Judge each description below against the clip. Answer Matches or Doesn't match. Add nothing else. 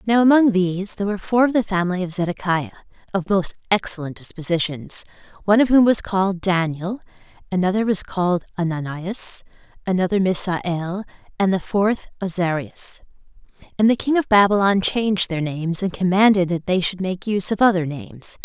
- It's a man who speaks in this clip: Doesn't match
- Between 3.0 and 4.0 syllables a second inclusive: Doesn't match